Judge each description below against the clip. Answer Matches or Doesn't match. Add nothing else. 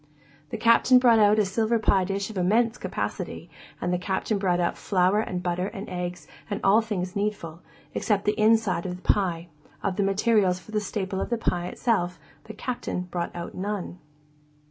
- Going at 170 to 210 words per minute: Matches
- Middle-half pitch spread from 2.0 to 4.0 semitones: Matches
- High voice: Matches